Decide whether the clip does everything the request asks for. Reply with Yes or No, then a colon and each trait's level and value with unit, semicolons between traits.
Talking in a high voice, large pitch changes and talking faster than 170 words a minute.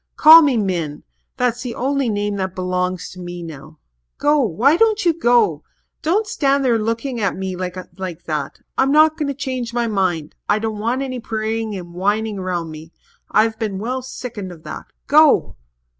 Yes: high, 220 Hz; wide, 6.1 semitones; average, 180 wpm